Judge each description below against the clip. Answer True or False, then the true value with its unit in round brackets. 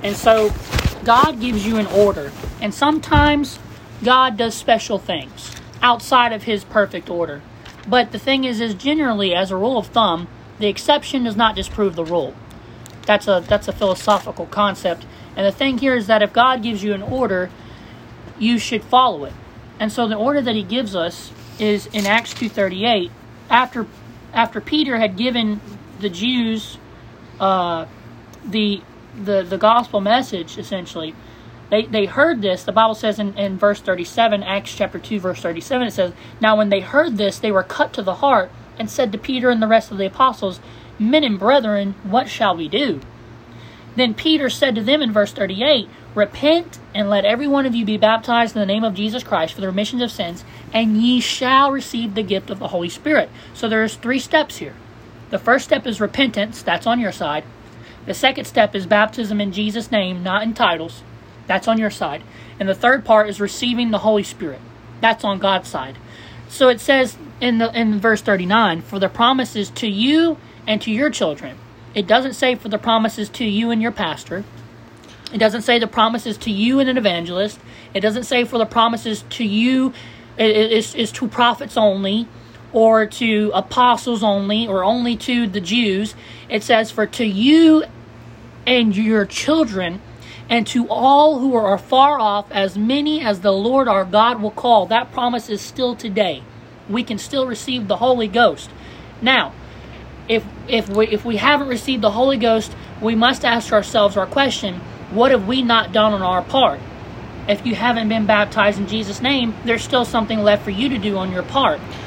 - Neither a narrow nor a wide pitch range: True (3.4 semitones)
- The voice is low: False (220 Hz)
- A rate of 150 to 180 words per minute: False (190 wpm)